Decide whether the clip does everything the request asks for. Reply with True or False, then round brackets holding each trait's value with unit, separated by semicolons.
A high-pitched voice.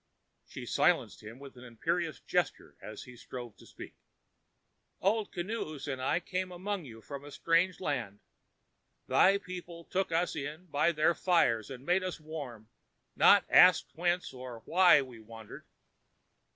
False (155 Hz)